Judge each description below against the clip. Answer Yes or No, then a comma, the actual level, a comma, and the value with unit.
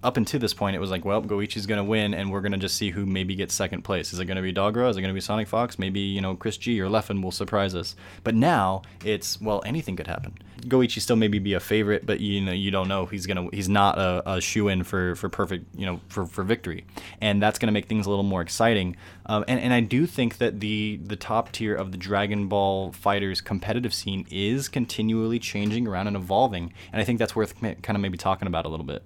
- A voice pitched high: No, low, 100 Hz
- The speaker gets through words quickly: Yes, fast, 255 wpm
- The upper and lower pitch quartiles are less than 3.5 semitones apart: Yes, narrow, 2.5 semitones